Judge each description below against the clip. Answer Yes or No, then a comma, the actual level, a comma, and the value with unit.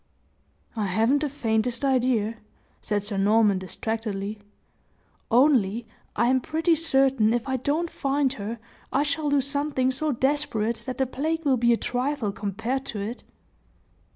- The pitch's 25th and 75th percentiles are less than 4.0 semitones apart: No, average, 4.3 semitones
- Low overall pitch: No, very high, 250 Hz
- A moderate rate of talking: Yes, average, 150 wpm